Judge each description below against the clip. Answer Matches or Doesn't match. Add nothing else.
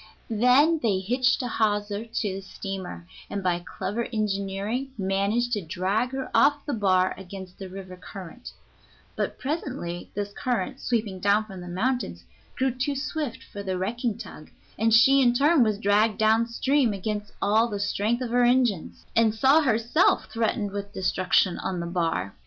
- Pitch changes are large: Doesn't match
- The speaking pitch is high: Matches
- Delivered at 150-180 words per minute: Matches